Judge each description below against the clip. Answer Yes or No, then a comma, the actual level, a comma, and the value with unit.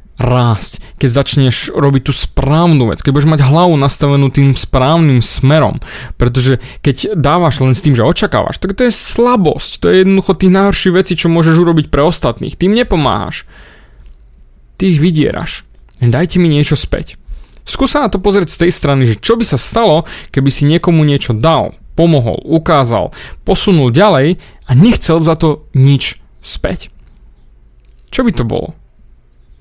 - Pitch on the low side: No, medium, 145 Hz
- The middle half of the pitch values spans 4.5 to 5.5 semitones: Yes, average, 5.2 semitones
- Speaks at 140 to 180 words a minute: Yes, average, 160 wpm